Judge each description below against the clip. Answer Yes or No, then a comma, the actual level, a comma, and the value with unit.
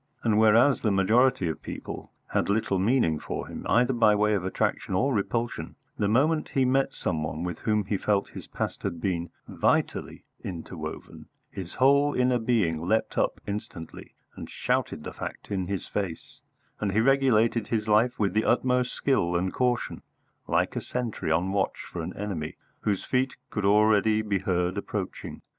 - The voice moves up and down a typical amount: Yes, average, 4.4 semitones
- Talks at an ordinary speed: Yes, average, 175 wpm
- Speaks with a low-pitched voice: Yes, low, 105 Hz